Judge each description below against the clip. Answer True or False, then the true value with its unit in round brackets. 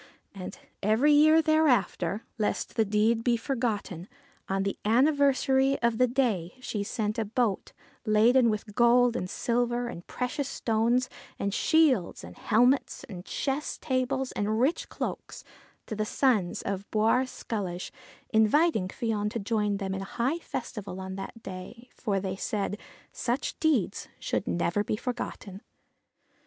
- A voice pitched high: True (225 Hz)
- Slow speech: False (145 wpm)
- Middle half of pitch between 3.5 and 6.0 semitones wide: True (4.1 semitones)